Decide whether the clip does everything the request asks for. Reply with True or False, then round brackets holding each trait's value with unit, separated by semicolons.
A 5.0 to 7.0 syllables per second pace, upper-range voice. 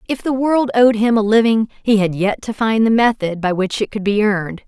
True (5.3 syllables/s; 215 Hz)